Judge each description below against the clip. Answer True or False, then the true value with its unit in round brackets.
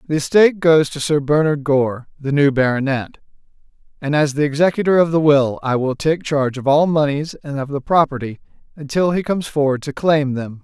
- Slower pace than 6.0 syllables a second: True (5.5 syllables/s)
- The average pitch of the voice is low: False (145 Hz)